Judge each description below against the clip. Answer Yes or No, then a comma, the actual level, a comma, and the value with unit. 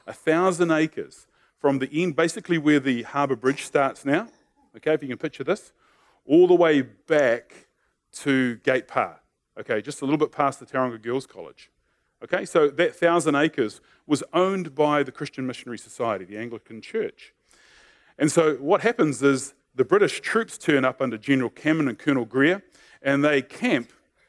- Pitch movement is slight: No, average, 4.5 semitones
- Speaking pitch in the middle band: Yes, medium, 150 Hz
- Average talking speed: Yes, average, 175 wpm